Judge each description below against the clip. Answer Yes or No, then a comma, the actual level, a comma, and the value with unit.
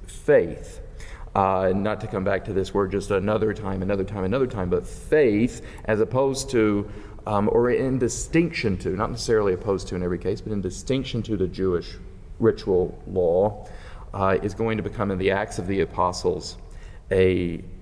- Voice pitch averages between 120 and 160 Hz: No, low, 100 Hz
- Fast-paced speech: No, average, 180 wpm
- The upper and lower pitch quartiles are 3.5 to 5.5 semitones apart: No, average, 2.8 semitones